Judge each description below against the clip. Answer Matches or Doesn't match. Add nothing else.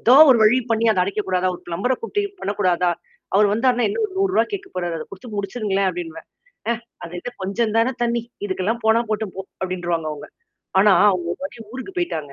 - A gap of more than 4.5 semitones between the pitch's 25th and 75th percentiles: Matches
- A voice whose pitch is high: Matches